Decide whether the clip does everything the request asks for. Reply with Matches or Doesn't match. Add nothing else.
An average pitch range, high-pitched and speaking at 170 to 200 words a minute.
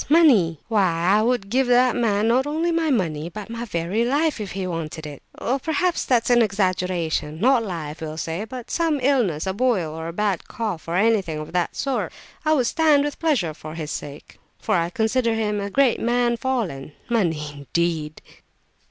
Doesn't match